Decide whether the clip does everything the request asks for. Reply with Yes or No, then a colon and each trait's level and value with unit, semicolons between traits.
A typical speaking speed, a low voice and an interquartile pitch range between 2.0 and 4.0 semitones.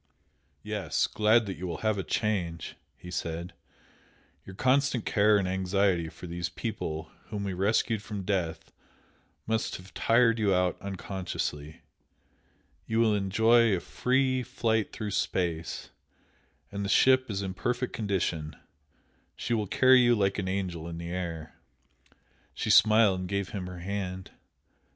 Yes: average, 145 wpm; low, 100 Hz; average, 3.6 semitones